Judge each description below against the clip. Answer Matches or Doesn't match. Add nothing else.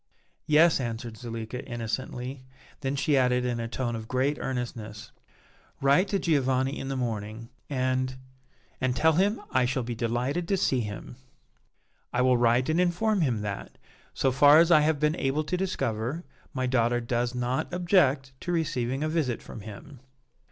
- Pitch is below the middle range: Matches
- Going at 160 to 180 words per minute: Matches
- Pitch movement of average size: Matches